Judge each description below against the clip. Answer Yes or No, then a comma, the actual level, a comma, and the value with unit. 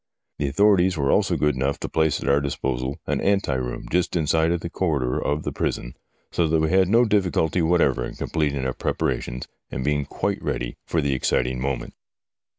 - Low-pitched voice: Yes, very low, 75 Hz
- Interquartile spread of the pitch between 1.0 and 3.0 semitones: No, average, 4.5 semitones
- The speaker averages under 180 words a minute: No, average, 195 wpm